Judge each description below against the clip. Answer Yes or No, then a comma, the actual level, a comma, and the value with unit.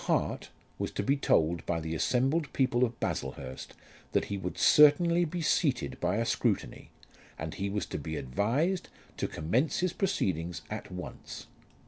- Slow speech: No, average, 160 wpm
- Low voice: Yes, low, 110 Hz